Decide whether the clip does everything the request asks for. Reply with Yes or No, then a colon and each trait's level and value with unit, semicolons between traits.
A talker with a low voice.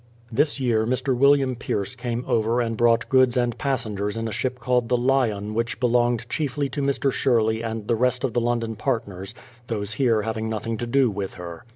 Yes: low, 120 Hz